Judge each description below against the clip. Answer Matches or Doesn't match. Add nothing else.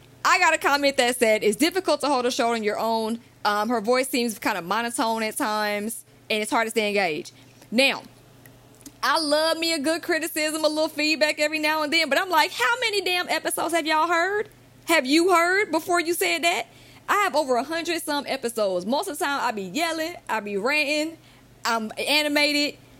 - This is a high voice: Matches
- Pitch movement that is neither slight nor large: Doesn't match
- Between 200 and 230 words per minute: Matches